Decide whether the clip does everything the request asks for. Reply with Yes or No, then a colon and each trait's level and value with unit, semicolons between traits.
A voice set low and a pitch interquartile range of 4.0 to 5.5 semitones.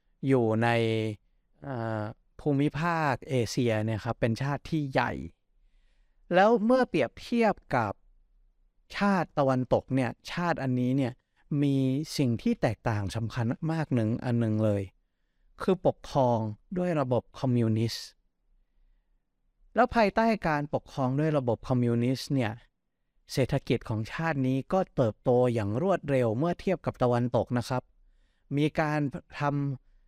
Yes: low, 130 Hz; average, 4.7 semitones